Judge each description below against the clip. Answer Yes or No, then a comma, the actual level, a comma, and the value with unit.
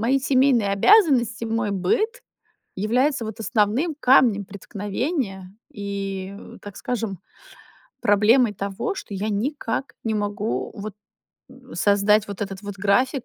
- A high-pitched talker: Yes, high, 210 Hz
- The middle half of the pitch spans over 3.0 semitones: Yes, average, 3.9 semitones